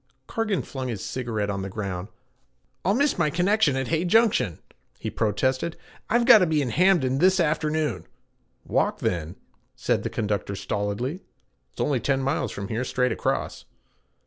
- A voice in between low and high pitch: No, low, 130 Hz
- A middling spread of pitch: No, wide, 8.8 semitones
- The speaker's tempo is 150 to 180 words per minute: Yes, average, 155 wpm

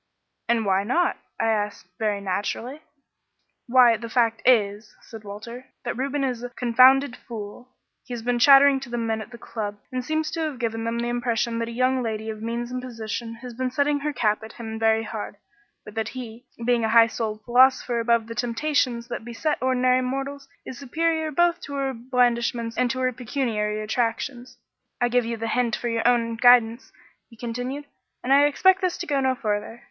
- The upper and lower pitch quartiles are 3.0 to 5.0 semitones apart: No, narrow, 2.4 semitones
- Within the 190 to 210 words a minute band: Yes, average, 195 wpm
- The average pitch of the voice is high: Yes, high, 240 Hz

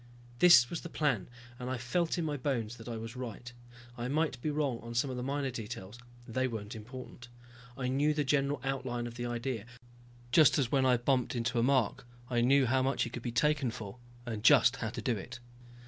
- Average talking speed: No, fast, 220 wpm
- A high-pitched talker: No, low, 125 Hz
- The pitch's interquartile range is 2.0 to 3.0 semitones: Yes, average, 2.7 semitones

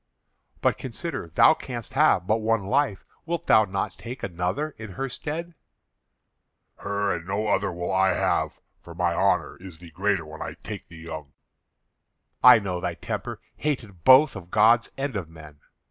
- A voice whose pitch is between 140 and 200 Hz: No, low, 100 Hz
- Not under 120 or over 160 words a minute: No, average, 170 wpm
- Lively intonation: Yes, wide, 6.0 semitones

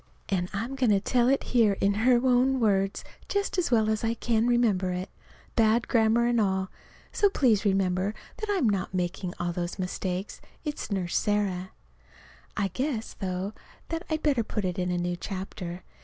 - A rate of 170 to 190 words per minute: Yes, average, 185 wpm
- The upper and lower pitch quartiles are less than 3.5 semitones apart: No, average, 4.4 semitones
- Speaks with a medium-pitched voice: No, high, 210 Hz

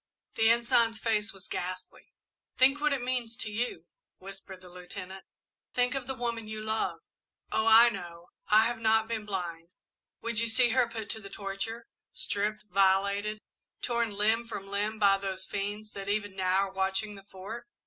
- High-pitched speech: Yes, high, 215 Hz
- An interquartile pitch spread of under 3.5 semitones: Yes, average, 2.9 semitones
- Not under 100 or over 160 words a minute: No, average, 175 wpm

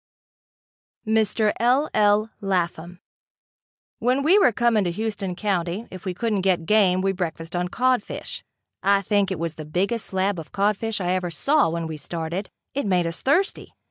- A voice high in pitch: Yes, high, 195 Hz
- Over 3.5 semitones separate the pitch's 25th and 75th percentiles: Yes, average, 3.9 semitones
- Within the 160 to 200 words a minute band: Yes, average, 170 wpm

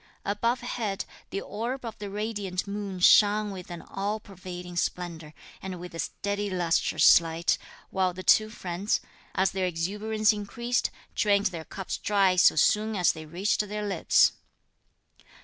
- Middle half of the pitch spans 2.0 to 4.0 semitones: Yes, average, 2.8 semitones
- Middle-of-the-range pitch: No, high, 195 Hz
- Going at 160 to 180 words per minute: No, average, 150 wpm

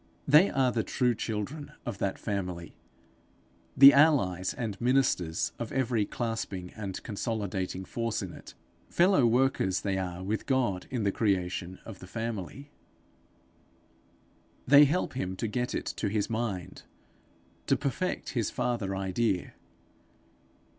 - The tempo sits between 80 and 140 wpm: Yes, slow, 135 wpm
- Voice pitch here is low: Yes, low, 110 Hz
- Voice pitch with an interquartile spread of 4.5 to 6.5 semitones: Yes, average, 4.9 semitones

